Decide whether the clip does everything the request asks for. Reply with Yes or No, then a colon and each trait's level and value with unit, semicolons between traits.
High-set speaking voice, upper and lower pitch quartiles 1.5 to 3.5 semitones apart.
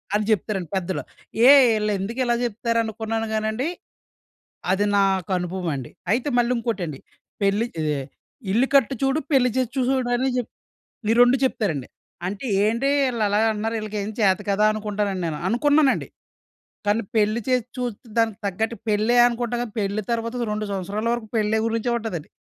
Yes: high, 220 Hz; average, 3.2 semitones